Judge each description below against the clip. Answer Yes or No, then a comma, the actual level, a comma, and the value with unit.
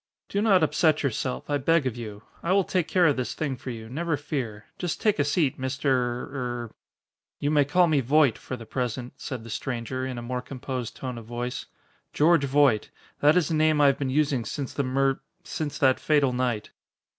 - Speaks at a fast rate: Yes, fast, 215 wpm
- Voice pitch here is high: No, low, 135 Hz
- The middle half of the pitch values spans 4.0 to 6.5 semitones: No, average, 3.5 semitones